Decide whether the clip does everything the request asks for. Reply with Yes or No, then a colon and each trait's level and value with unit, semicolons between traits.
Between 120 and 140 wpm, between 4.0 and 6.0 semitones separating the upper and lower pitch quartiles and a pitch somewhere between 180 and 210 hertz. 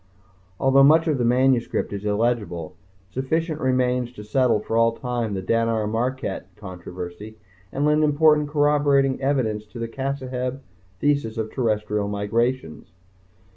No: slow, 135 wpm; average, 4.4 semitones; low, 120 Hz